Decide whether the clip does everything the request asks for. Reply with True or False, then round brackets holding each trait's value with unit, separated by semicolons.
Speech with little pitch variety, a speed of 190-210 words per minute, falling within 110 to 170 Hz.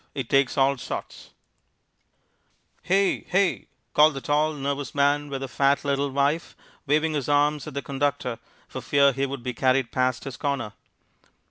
False (1.6 semitones; 160 wpm; 140 Hz)